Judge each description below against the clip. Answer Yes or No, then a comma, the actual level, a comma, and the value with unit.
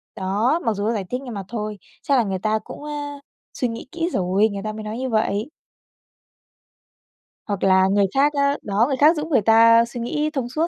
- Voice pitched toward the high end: Yes, high, 230 Hz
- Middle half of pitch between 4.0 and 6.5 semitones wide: Yes, average, 5.0 semitones